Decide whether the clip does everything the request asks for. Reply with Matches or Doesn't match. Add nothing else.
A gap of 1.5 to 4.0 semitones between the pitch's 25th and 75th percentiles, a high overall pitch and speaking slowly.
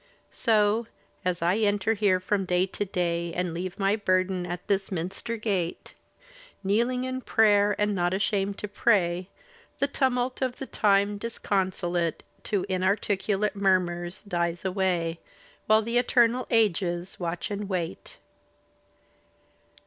Matches